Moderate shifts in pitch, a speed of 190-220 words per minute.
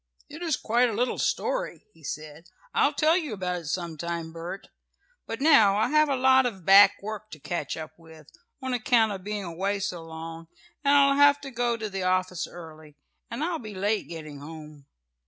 No: wide, 7.1 semitones; average, 200 wpm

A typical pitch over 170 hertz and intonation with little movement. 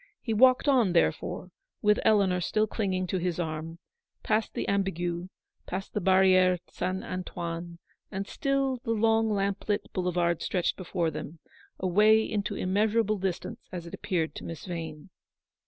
No: high, 190 Hz; average, 3.5 semitones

